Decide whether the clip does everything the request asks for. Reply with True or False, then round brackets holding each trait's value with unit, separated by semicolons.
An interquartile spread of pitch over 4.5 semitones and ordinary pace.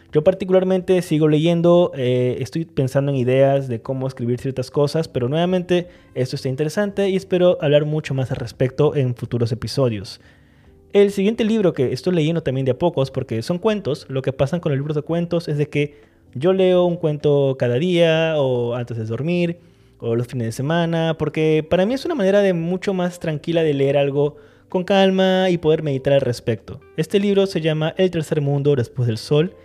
False (5.0 semitones; 200 wpm)